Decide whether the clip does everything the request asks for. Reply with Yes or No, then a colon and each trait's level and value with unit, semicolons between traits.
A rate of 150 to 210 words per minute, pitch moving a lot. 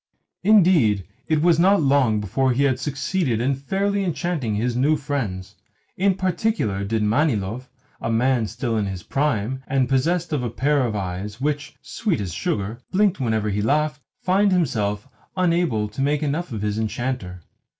Yes: average, 165 wpm; wide, 6.9 semitones